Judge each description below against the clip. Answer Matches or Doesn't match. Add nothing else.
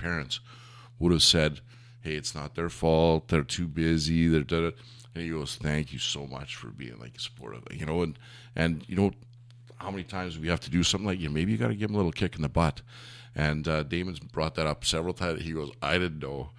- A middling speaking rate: Doesn't match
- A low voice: Matches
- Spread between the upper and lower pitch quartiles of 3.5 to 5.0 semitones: Matches